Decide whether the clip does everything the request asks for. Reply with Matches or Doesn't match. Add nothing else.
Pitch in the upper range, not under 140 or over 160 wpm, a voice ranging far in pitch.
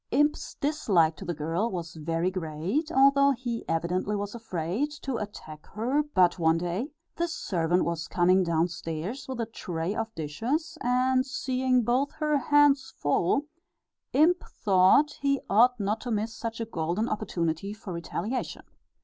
Matches